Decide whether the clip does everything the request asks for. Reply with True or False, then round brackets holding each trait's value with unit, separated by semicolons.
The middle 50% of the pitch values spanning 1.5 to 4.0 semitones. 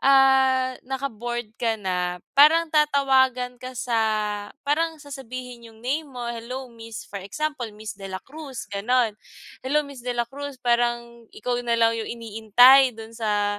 True (2.9 semitones)